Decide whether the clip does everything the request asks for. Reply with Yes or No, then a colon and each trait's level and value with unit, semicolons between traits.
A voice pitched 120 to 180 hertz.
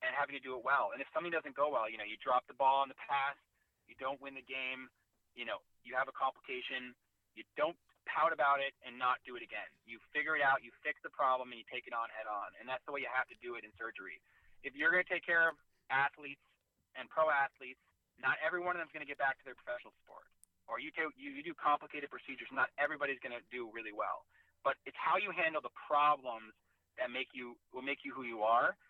Yes: medium, 140 Hz